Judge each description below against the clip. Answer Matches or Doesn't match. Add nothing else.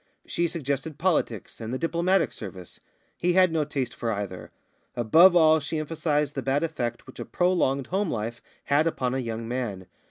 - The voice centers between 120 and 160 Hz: Matches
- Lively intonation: Matches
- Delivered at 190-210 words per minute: Doesn't match